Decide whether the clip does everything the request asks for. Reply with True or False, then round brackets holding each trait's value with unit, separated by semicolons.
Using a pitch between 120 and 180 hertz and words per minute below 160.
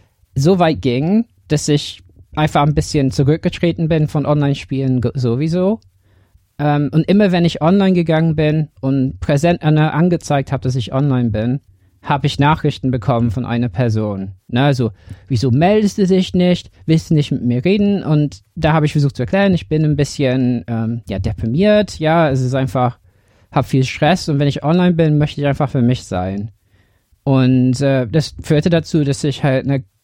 False (140 Hz; 180 wpm)